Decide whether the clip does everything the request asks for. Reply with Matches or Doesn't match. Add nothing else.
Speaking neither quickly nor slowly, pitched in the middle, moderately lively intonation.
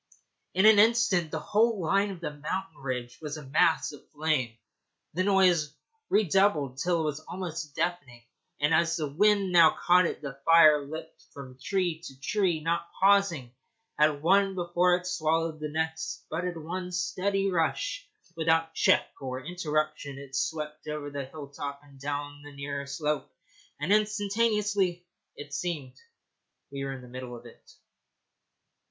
Matches